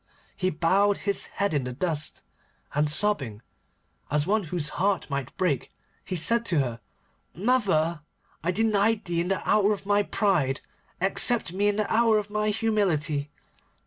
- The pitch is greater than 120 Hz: Yes, high, 190 Hz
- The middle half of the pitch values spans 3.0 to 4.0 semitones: No, wide, 5.4 semitones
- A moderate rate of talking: Yes, average, 160 wpm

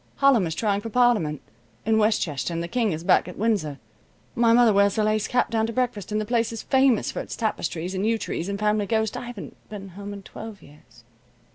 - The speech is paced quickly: Yes, fast, 230 wpm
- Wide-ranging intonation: No, average, 3.2 semitones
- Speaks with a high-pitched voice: Yes, high, 210 Hz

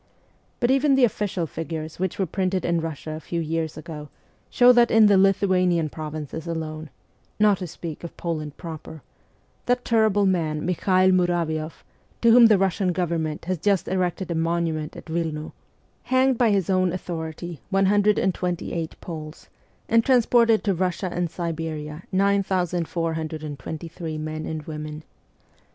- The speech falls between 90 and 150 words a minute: Yes, average, 140 wpm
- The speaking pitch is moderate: Yes, medium, 170 Hz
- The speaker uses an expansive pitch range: No, average, 3.5 semitones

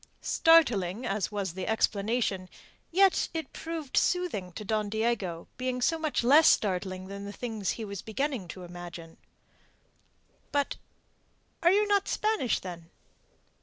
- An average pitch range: No, wide, 7.6 semitones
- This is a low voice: No, high, 220 Hz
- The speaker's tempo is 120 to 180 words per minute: Yes, slow, 135 wpm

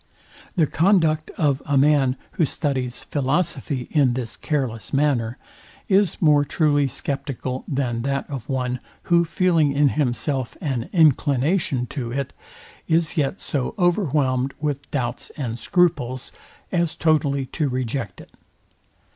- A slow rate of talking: Yes, slow, 130 wpm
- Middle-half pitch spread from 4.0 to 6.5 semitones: No, average, 3.3 semitones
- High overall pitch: No, medium, 140 Hz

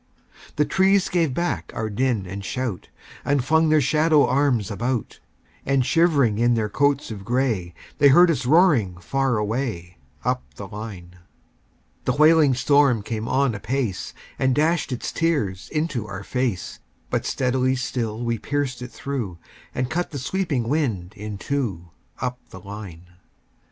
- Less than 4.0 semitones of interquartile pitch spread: No, average, 5.3 semitones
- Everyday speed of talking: Yes, average, 150 wpm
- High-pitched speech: No, low, 125 Hz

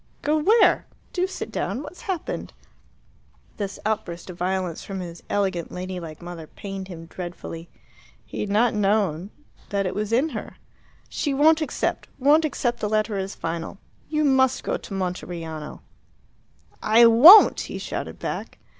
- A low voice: No, high, 200 Hz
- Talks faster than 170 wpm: No, average, 150 wpm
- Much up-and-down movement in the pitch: Yes, wide, 6.8 semitones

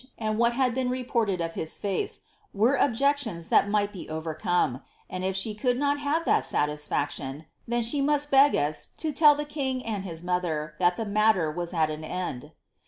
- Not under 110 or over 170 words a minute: No, average, 195 wpm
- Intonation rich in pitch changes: Yes, wide, 7.7 semitones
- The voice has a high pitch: Yes, high, 205 Hz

